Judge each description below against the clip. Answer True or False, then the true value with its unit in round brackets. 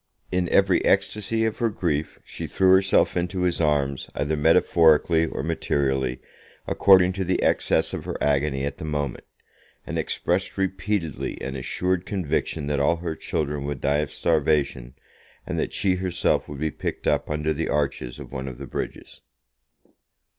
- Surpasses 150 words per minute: True (165 wpm)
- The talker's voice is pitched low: True (80 Hz)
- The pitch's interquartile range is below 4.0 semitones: False (4.4 semitones)